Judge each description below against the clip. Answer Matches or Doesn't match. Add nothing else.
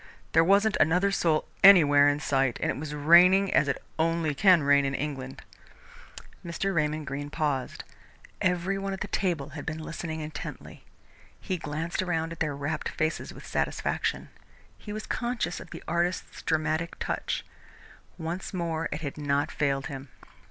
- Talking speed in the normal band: Matches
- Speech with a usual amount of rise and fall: Matches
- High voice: Doesn't match